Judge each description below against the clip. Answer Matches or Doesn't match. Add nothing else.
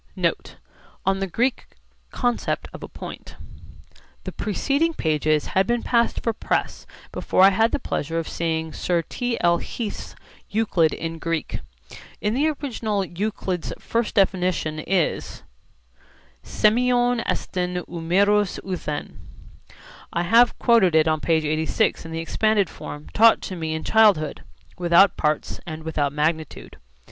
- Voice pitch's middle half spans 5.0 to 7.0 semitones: Matches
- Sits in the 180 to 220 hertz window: Matches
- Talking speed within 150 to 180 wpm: Doesn't match